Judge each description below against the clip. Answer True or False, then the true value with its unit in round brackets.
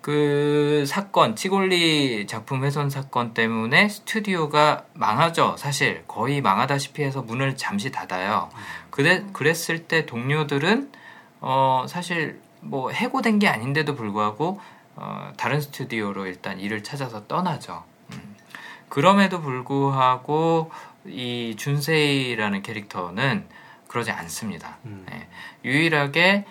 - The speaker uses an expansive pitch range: False (4.7 semitones)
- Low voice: False (145 Hz)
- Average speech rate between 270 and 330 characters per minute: False (260 characters per minute)